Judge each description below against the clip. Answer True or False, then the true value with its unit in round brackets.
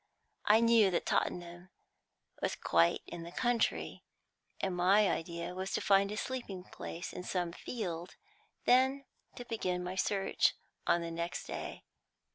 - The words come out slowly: False (145 wpm)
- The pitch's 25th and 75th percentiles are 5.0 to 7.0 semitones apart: False (4.0 semitones)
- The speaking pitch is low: False (185 Hz)